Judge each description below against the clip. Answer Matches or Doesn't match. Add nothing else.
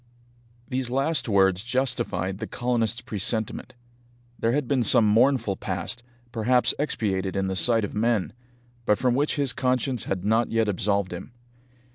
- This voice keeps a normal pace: Matches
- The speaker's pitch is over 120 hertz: Doesn't match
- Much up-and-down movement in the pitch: Doesn't match